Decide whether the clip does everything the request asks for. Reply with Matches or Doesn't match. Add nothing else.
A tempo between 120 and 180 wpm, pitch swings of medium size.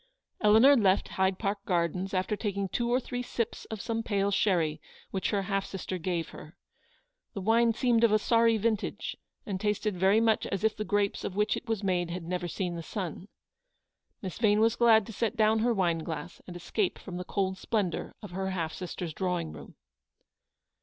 Doesn't match